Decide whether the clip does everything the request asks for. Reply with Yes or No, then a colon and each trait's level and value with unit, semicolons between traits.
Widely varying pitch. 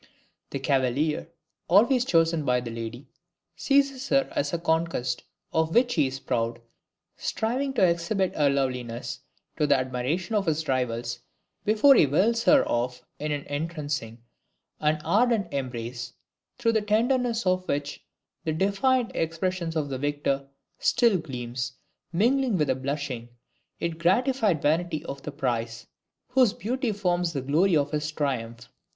Yes: wide, 7.7 semitones